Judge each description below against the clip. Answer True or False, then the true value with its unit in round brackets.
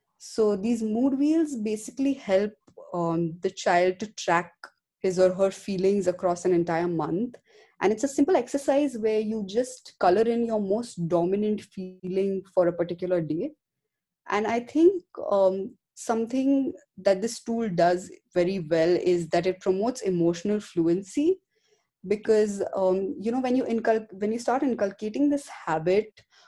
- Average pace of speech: True (150 wpm)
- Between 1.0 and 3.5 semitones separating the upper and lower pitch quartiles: False (5.0 semitones)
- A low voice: False (210 Hz)